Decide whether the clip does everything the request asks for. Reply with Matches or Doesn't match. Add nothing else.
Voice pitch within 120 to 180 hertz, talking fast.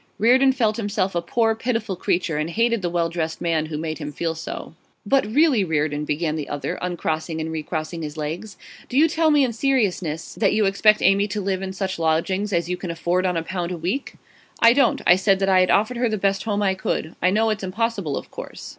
Doesn't match